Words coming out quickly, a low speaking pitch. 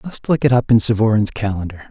Yes: fast, 250 wpm; low, 115 Hz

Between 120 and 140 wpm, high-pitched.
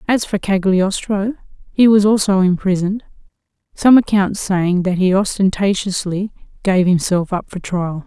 Yes: slow, 135 wpm; high, 195 Hz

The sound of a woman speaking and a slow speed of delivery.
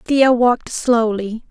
Yes: female; slow, 120 wpm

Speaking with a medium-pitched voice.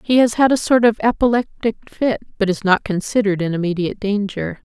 No: high, 210 Hz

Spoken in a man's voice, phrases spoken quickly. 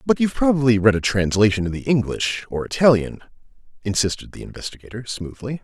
No: male; average, 160 wpm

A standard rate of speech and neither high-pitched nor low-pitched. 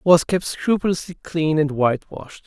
Yes: average, 170 wpm; medium, 160 Hz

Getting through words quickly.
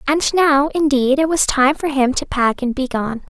Yes: fast, 215 wpm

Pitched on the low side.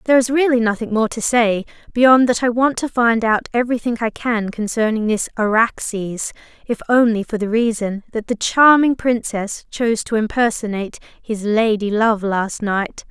No: high, 225 Hz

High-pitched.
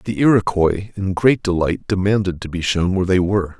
No: very low, 95 Hz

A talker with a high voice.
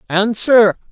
Yes: high, 215 Hz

